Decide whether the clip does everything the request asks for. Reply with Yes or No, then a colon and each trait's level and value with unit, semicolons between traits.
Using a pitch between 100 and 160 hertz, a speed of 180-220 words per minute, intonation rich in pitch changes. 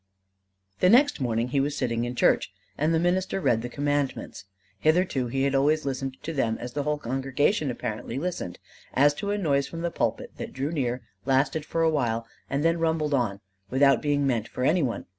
No: medium, 140 Hz; average, 200 wpm; average, 3.9 semitones